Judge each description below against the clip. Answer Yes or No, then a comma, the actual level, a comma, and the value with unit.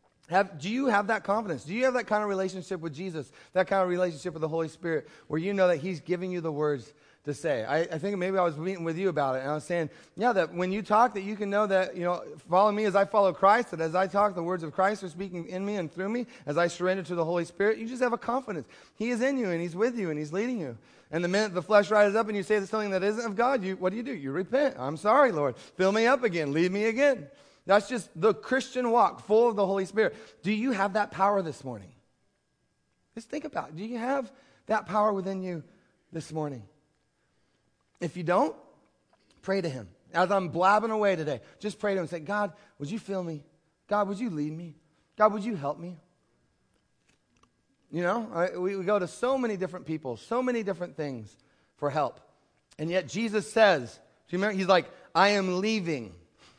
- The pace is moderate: No, fast, 245 wpm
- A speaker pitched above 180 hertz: Yes, high, 190 Hz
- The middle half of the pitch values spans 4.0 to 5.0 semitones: Yes, average, 4.6 semitones